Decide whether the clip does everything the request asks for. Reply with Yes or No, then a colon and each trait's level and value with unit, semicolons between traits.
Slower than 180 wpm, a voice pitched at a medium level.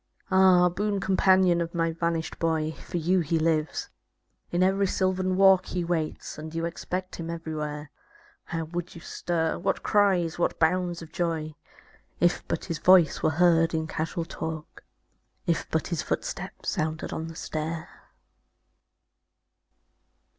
Yes: average, 145 wpm; medium, 170 Hz